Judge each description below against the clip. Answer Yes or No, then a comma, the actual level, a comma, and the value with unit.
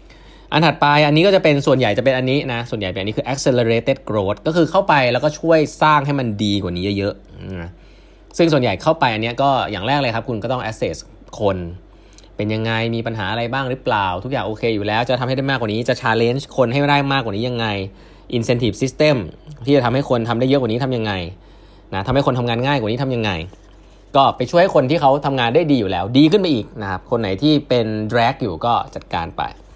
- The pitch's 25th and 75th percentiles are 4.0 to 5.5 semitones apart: Yes, average, 4.6 semitones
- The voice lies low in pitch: Yes, low, 125 Hz